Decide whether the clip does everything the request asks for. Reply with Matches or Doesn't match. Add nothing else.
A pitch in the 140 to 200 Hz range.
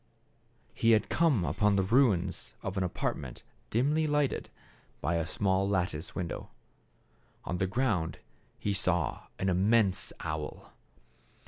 Doesn't match